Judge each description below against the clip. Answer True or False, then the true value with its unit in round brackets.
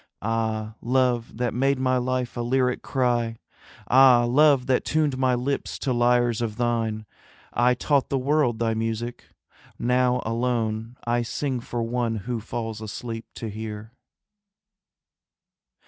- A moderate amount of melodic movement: False (2.0 semitones)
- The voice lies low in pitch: True (120 Hz)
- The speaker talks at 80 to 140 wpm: True (135 wpm)